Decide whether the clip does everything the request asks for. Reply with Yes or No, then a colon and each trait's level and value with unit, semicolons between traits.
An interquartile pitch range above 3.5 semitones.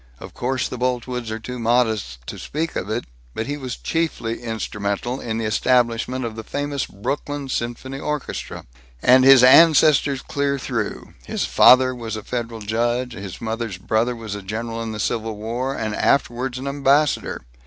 No: average, 2.9 semitones